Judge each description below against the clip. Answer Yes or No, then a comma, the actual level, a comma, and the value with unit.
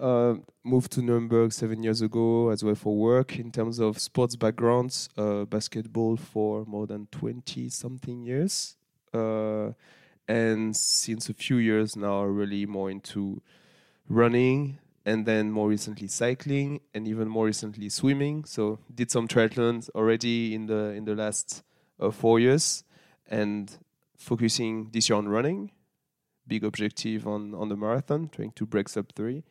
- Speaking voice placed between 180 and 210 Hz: No, low, 110 Hz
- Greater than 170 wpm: No, average, 155 wpm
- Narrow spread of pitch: Yes, narrow, 2.3 semitones